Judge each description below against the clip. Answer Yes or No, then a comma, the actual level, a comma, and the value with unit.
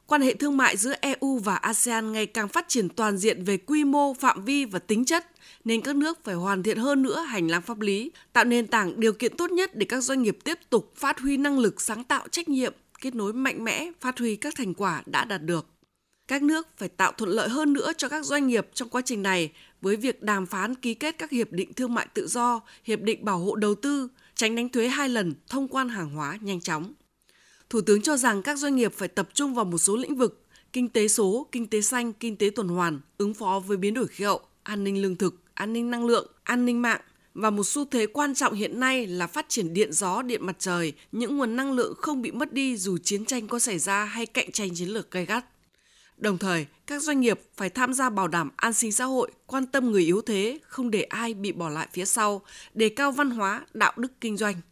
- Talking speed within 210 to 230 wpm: No, fast, 250 wpm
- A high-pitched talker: Yes, high, 230 Hz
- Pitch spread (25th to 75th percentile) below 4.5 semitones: No, average, 4.8 semitones